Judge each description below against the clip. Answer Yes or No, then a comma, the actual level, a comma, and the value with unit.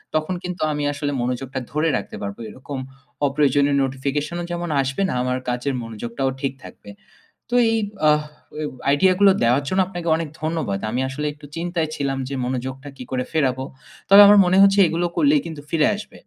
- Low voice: No, medium, 145 Hz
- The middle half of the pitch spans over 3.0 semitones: Yes, average, 4.2 semitones